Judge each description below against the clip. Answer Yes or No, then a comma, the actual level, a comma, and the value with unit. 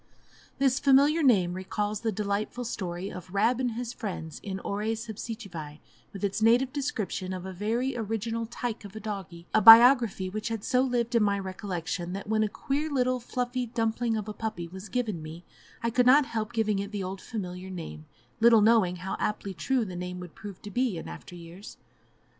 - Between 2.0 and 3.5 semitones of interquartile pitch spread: No, average, 4.0 semitones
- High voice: Yes, high, 215 Hz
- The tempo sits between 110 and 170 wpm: No, average, 195 wpm